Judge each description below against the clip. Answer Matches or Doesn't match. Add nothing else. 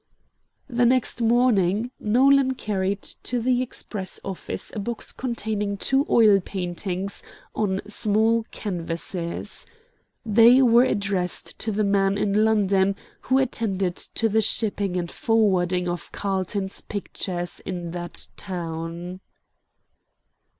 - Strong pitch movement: Doesn't match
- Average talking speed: Doesn't match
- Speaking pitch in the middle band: Doesn't match